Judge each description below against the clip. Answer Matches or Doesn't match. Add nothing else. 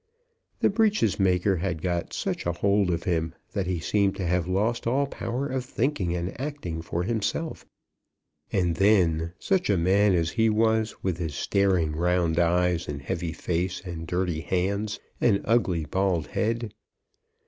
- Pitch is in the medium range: Doesn't match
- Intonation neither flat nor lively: Matches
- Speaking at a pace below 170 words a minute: Matches